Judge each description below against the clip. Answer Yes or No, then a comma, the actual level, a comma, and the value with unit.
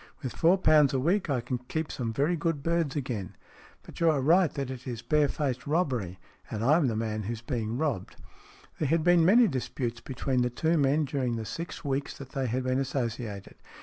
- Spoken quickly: Yes, fast, 215 wpm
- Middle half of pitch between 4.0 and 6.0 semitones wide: Yes, average, 4.5 semitones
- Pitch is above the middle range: No, low, 135 Hz